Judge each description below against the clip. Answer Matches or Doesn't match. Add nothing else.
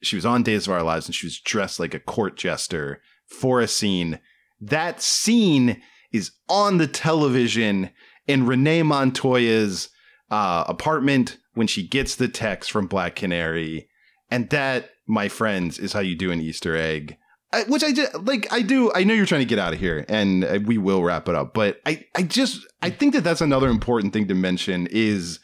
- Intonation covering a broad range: Matches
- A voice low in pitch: Matches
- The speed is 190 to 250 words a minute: Matches